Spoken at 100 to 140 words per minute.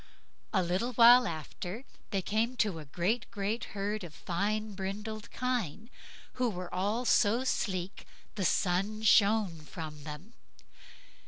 Yes: slow, 135 wpm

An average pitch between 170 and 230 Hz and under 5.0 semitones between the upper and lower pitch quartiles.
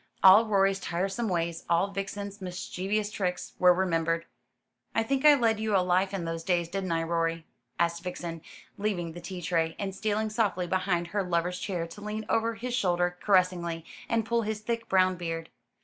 Yes: medium, 185 Hz; average, 3.5 semitones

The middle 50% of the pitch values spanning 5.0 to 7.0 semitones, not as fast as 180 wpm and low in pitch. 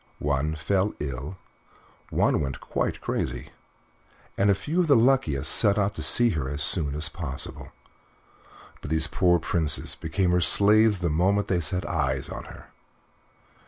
Yes: average, 5.3 semitones; average, 160 wpm; very low, 85 Hz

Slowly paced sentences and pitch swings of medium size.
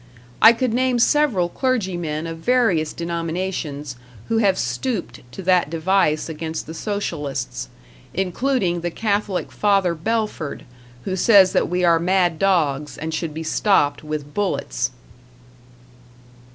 Yes: slow, 125 wpm; average, 4.3 semitones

